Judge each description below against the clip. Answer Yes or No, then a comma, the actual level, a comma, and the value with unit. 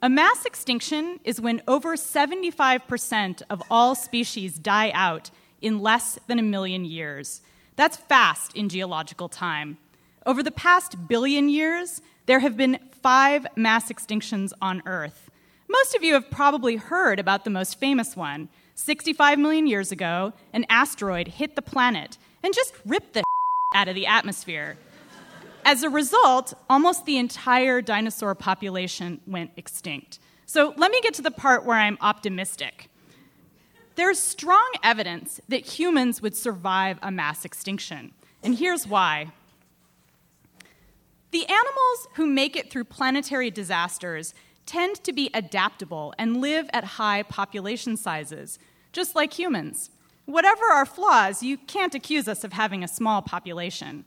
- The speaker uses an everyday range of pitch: No, wide, 7.7 semitones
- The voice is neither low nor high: No, high, 235 Hz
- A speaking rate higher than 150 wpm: No, average, 145 wpm